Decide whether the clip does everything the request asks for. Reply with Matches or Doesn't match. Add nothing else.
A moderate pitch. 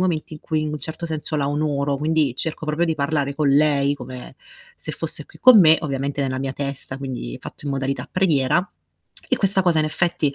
Matches